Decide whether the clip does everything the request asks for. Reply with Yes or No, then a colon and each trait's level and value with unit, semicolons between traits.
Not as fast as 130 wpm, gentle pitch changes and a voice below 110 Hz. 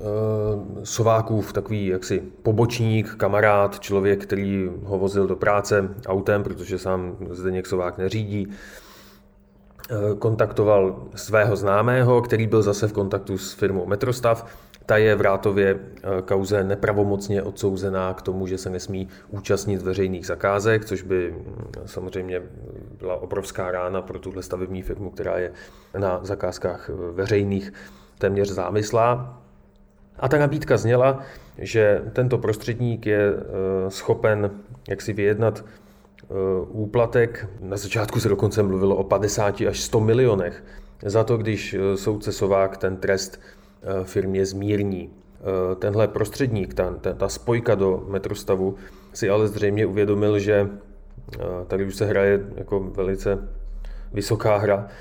Yes: average, 120 wpm; narrow, 1.9 semitones; low, 100 Hz